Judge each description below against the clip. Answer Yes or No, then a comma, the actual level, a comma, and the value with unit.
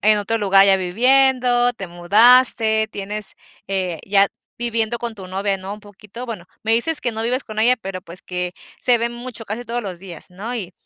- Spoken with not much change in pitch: No, average, 3.7 semitones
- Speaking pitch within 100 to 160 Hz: No, high, 215 Hz